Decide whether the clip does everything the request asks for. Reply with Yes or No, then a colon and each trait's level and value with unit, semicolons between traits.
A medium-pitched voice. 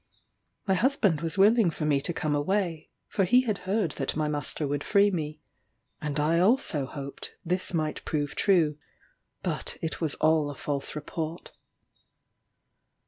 Yes: medium, 160 Hz